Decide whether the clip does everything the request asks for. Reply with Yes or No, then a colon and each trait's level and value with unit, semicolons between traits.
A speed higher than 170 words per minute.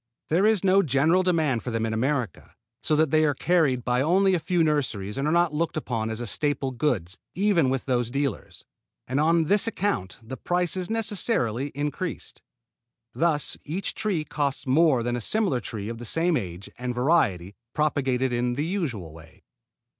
Yes: average, 180 wpm